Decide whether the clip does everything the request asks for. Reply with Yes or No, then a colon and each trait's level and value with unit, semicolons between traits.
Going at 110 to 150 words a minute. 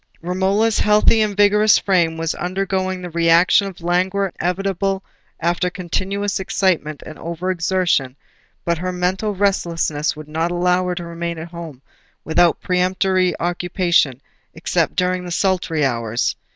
Yes: average, 140 wpm